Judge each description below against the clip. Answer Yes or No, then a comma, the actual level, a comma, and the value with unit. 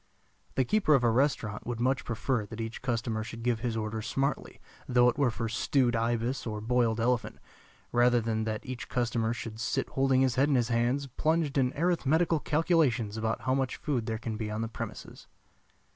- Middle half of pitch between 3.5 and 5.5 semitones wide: No, average, 2.9 semitones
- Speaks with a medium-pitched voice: No, low, 120 Hz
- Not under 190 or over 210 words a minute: Yes, average, 195 wpm